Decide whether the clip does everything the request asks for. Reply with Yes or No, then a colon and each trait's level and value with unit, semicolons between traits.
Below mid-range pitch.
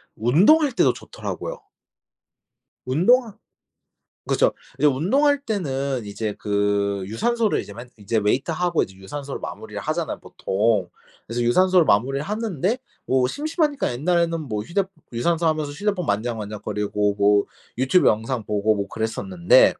Yes: low, 130 Hz